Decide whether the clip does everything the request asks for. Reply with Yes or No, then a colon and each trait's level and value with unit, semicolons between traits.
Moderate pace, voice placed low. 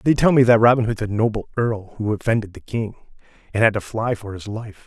No: fast, 245 wpm; low, 110 Hz